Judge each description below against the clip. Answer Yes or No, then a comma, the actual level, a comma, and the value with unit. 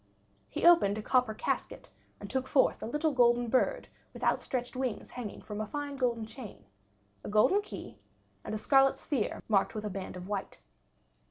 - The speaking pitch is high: Yes, high, 240 Hz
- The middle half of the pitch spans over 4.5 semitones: No, average, 4.2 semitones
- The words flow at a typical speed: Yes, average, 180 wpm